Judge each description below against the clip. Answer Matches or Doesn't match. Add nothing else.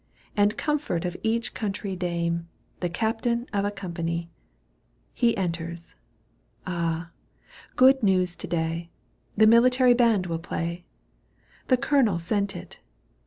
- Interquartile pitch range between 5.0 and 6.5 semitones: Matches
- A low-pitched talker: Doesn't match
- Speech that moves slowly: Matches